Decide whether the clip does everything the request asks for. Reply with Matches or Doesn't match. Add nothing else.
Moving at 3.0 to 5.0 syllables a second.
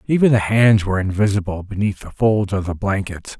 Doesn't match